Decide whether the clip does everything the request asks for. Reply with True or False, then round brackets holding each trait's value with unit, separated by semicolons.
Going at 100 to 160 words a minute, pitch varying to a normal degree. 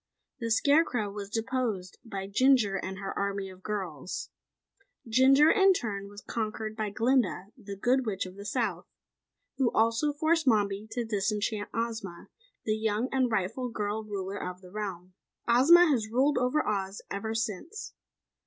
True (155 wpm; 4.0 semitones)